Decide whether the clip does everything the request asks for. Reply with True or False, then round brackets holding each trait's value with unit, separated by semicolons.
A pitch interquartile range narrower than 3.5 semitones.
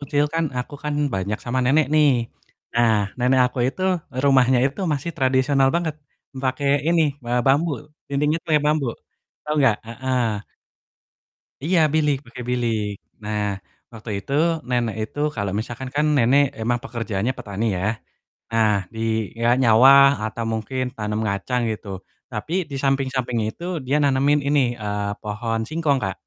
False (4.1 semitones)